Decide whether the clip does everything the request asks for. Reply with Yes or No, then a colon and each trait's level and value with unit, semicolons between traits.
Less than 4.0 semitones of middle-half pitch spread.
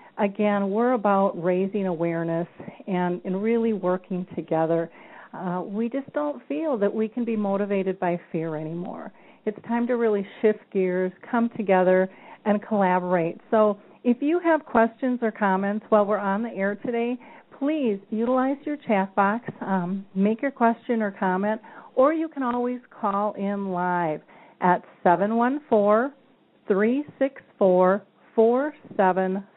No: average, 4.3 semitones